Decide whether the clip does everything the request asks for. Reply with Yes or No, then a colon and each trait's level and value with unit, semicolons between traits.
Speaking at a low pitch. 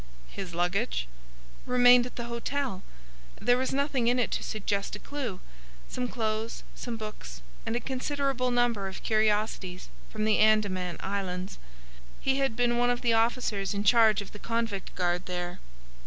No: high, 220 Hz